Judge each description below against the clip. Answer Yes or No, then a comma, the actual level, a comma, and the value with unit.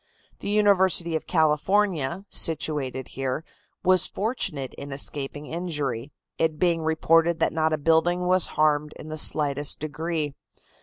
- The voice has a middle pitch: Yes, medium, 160 Hz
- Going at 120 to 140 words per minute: Yes, slow, 135 wpm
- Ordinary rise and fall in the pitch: Yes, average, 3.0 semitones